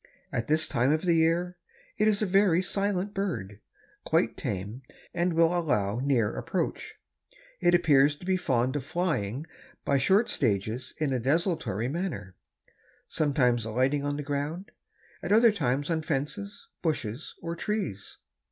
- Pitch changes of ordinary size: No, wide, 6.2 semitones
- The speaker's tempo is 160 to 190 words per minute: No, average, 150 wpm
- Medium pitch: Yes, medium, 150 Hz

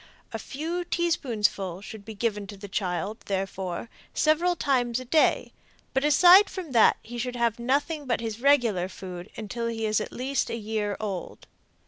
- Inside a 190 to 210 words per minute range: No, average, 170 wpm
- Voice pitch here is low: No, high, 230 Hz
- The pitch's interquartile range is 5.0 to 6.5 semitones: Yes, average, 5.3 semitones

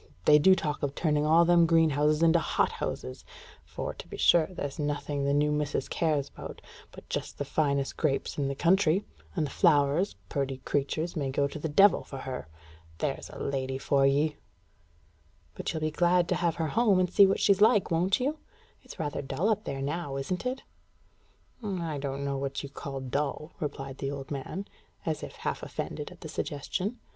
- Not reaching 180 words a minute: No, average, 190 wpm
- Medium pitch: Yes, medium, 150 Hz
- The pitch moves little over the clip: No, average, 3.7 semitones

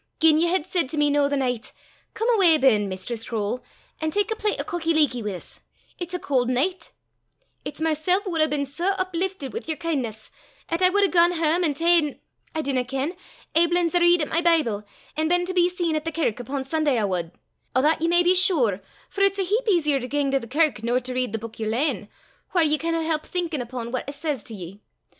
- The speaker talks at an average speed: No, fast, 240 wpm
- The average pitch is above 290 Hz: Yes, very high, 310 Hz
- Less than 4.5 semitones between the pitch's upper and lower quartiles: No, wide, 5.4 semitones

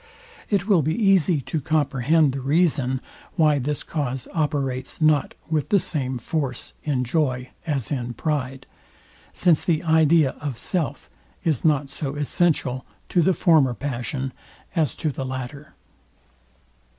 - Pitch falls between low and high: Yes, medium, 145 Hz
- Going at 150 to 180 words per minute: No, average, 140 wpm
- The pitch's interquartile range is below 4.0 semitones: Yes, average, 3.4 semitones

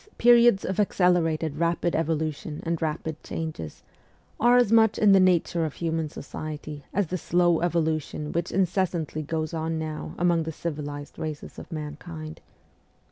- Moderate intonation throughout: No, narrow, 2.3 semitones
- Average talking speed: Yes, average, 150 wpm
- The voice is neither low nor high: Yes, medium, 165 Hz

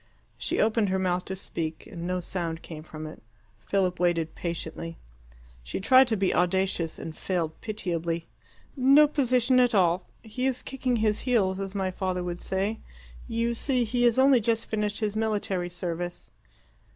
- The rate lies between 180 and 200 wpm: No, average, 165 wpm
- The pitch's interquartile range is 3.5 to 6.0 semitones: Yes, average, 4.7 semitones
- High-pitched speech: Yes, high, 195 Hz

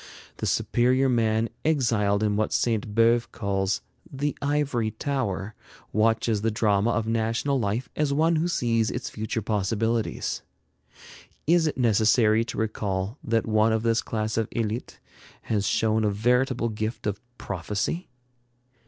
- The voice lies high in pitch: No, low, 115 Hz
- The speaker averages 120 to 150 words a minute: Yes, average, 140 wpm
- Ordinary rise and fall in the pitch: No, narrow, 2.3 semitones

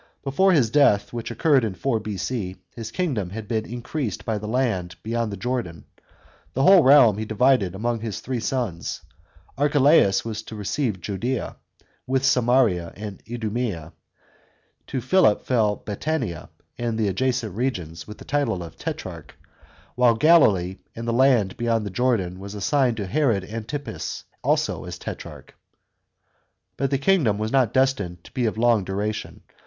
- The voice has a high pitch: No, low, 115 Hz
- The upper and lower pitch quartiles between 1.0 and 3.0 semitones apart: No, average, 4.4 semitones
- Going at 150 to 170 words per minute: Yes, average, 155 wpm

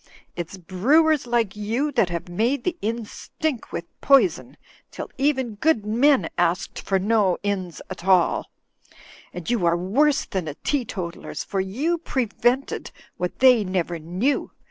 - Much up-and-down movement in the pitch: Yes, wide, 6.5 semitones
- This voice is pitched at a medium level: No, high, 210 Hz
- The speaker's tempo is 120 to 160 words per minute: Yes, average, 145 wpm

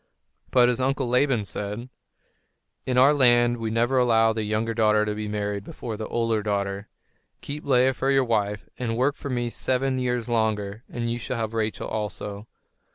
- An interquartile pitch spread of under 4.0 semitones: Yes, average, 2.8 semitones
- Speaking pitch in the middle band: No, low, 115 Hz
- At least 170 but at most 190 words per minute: Yes, average, 180 wpm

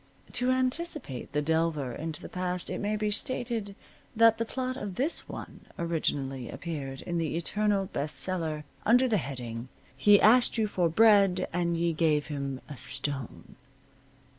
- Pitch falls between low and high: Yes, medium, 175 Hz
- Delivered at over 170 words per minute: No, average, 160 wpm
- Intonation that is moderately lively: No, wide, 6.4 semitones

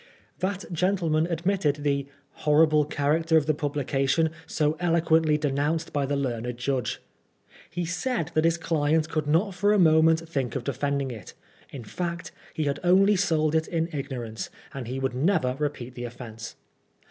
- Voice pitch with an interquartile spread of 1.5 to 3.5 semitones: Yes, average, 3.2 semitones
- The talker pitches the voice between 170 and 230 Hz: No, medium, 155 Hz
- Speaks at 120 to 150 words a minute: No, average, 170 wpm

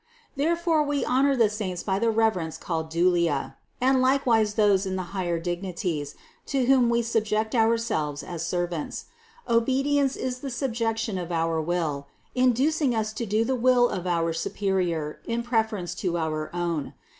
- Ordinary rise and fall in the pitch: No, wide, 6.0 semitones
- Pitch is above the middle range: Yes, high, 215 Hz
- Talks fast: No, average, 155 wpm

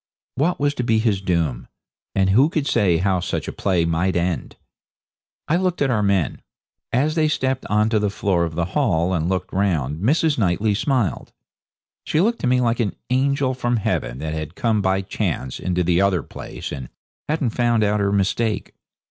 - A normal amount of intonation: No, wide, 6.1 semitones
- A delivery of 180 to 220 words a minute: Yes, average, 190 wpm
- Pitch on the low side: Yes, low, 100 Hz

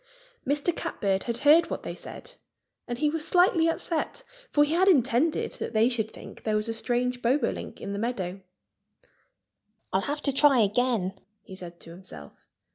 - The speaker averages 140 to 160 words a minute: No, average, 175 wpm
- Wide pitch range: Yes, wide, 6.5 semitones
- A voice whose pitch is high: Yes, high, 245 Hz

